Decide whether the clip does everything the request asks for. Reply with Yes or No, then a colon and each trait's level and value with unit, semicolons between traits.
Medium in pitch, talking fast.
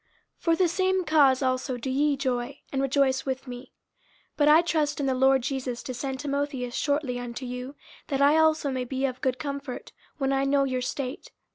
No: very high, 270 Hz; fast, 210 wpm